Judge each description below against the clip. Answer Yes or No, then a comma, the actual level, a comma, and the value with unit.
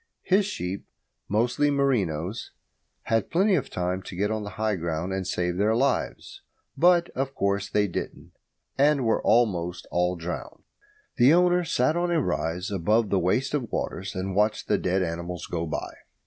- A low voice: Yes, low, 105 Hz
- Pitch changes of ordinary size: No, wide, 7.0 semitones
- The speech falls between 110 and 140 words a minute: No, average, 170 wpm